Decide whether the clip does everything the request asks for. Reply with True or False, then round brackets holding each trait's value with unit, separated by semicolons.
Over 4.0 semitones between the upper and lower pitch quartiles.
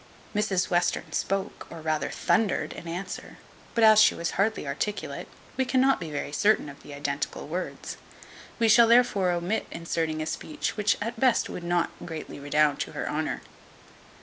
True (5.6 semitones)